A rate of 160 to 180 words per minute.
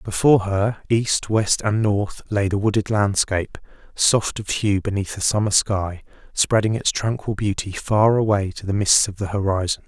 Yes: average, 175 wpm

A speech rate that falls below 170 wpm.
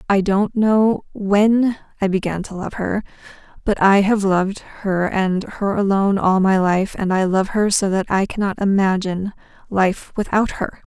No: average, 175 wpm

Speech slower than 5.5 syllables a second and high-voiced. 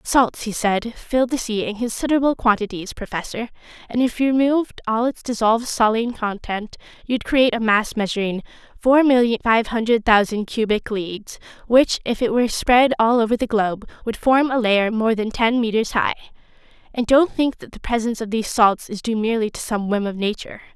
No: 5.6 syllables/s; high, 225 Hz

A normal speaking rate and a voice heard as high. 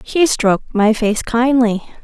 Yes: average, 145 wpm; high, 235 Hz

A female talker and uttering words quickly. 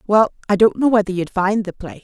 Yes: female; fast, 265 wpm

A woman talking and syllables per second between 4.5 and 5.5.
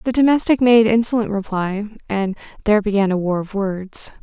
Yes: female; 5.3 syllables/s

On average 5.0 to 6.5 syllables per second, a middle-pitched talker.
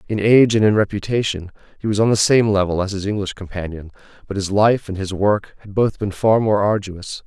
No: 5.6 syllables/s; low, 100 Hz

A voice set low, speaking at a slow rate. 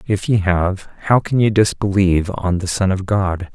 No: very low, 95 Hz; fast, 205 wpm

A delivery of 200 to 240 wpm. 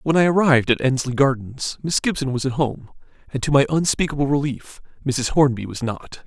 No: average, 190 wpm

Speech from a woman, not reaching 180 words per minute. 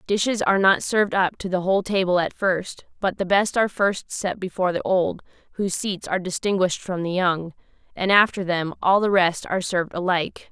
No: female; fast, 205 wpm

